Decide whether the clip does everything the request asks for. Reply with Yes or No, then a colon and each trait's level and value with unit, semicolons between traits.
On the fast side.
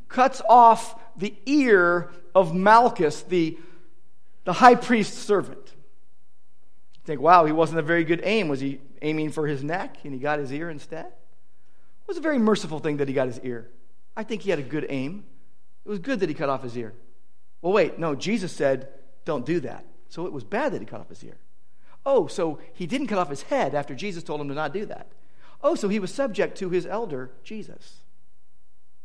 Yes: fast, 210 wpm